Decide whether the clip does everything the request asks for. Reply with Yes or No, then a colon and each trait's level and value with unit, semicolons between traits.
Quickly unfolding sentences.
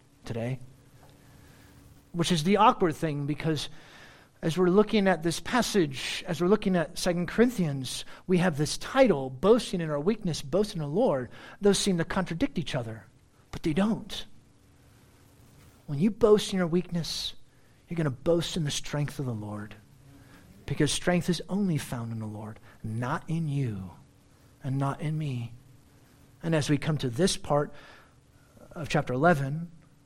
No: average, 160 wpm